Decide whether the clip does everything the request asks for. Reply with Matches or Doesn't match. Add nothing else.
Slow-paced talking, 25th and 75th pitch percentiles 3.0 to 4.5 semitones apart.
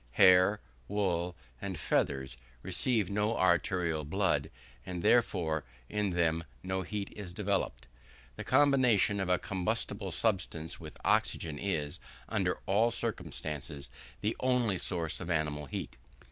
Matches